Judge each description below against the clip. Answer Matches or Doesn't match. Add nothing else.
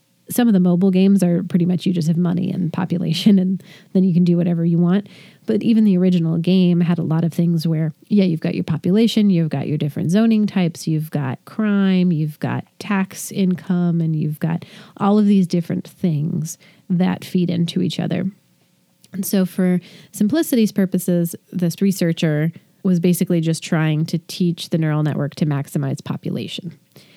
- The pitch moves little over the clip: Matches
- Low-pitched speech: Doesn't match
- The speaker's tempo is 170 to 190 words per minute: Matches